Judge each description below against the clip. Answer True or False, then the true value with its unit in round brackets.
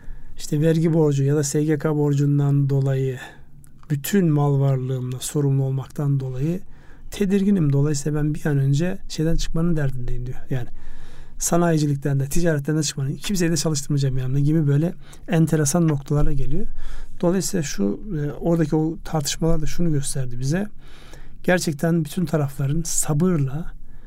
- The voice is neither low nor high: True (150 Hz)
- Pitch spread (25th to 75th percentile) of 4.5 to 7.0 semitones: False (3.0 semitones)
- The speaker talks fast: False (130 wpm)